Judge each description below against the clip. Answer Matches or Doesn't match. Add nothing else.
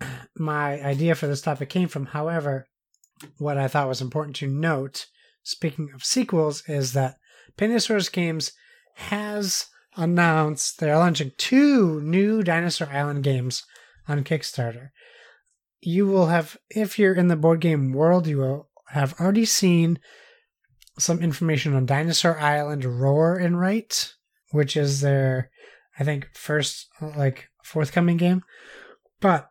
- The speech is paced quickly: Doesn't match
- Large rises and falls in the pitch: Doesn't match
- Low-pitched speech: Doesn't match